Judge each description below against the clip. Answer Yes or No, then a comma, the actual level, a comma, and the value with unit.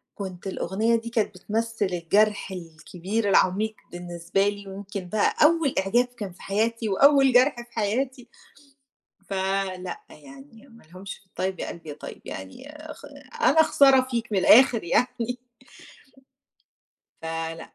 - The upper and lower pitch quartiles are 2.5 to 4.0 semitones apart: No, average, 4.4 semitones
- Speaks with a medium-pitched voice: No, high, 205 Hz